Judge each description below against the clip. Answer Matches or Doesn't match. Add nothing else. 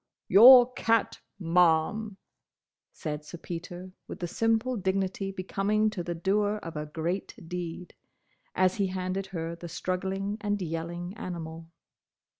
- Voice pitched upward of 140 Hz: Matches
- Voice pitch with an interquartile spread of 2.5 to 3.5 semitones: Matches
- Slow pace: Matches